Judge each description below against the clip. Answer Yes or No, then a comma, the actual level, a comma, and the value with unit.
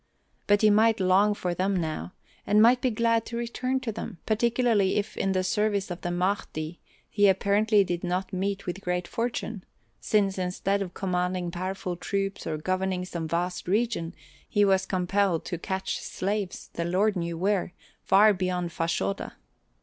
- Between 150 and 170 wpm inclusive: Yes, average, 165 wpm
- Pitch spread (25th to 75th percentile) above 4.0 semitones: No, narrow, 2.6 semitones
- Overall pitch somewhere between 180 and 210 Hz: Yes, high, 190 Hz